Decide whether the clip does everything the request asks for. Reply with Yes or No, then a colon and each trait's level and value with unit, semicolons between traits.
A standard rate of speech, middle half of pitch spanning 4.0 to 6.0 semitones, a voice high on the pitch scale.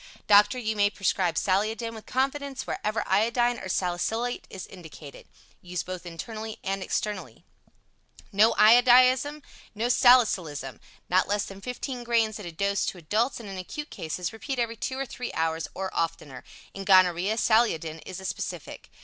Yes: average, 160 wpm; average, 4.6 semitones; high, 205 Hz